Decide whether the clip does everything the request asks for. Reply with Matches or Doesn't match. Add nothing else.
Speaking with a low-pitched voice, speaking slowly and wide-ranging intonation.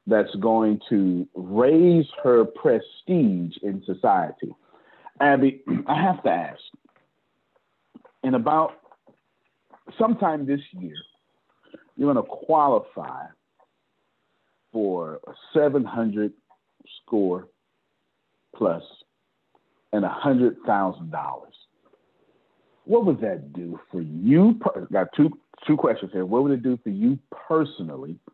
Matches